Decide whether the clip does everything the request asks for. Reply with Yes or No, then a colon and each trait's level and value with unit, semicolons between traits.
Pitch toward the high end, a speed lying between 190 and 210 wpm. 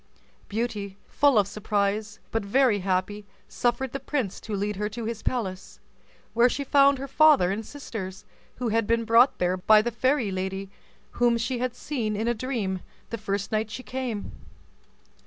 No: high, 220 Hz; average, 175 wpm